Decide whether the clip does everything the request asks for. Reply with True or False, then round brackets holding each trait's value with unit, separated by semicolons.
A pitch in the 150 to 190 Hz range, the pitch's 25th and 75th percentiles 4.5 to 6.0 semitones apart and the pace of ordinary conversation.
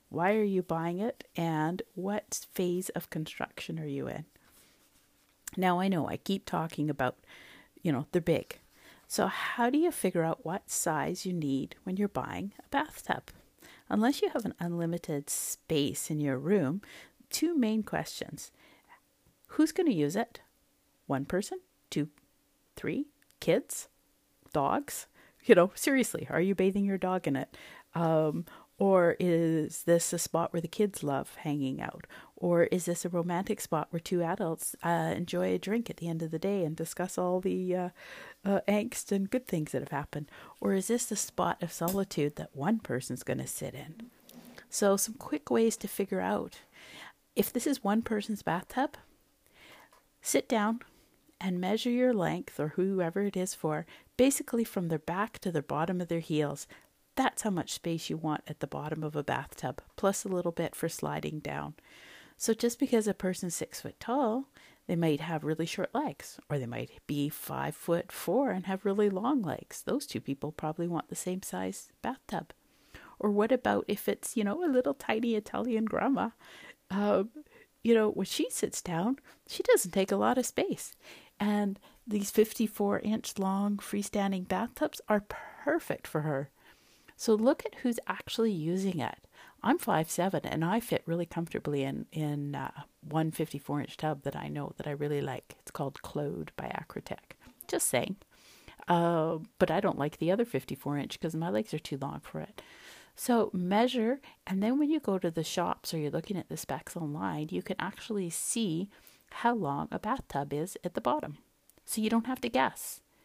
True (185 Hz; 5.5 semitones; 180 wpm)